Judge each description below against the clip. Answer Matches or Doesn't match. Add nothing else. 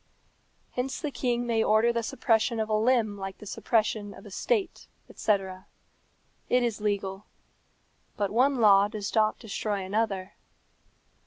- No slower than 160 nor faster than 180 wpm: Doesn't match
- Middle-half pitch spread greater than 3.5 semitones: Doesn't match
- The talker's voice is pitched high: Matches